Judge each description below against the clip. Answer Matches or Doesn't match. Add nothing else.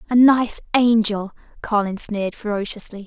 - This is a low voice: Doesn't match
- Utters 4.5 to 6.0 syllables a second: Matches